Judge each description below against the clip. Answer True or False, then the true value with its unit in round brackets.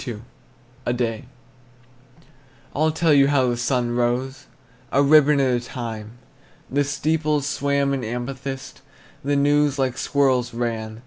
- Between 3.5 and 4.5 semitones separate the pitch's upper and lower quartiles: False (2.8 semitones)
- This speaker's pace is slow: True (130 wpm)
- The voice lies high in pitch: False (135 Hz)